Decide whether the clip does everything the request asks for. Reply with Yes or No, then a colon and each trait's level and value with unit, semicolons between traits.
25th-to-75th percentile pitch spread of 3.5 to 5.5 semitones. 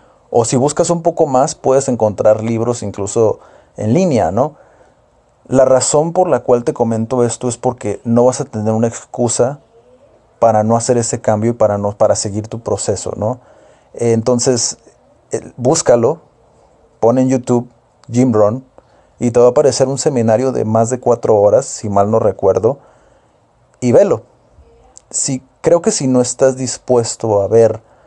No: narrow, 2.5 semitones